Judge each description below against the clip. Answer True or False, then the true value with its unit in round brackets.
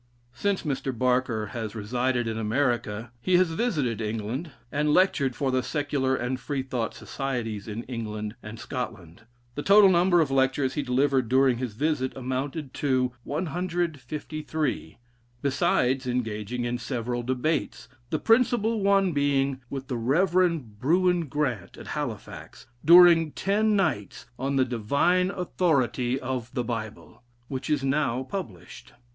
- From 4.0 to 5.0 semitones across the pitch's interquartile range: True (4.6 semitones)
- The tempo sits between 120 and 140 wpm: True (135 wpm)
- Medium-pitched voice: False (130 Hz)